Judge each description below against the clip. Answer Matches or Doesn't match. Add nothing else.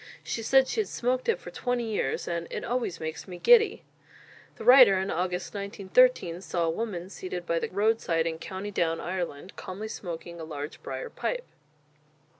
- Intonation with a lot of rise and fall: Matches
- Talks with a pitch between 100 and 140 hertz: Doesn't match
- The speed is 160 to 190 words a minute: Matches